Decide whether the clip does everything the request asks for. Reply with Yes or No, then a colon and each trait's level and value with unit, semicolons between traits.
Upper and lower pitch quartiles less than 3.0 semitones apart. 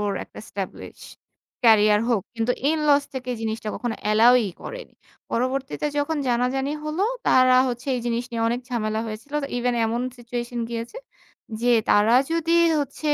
Yes: narrow, 2.6 semitones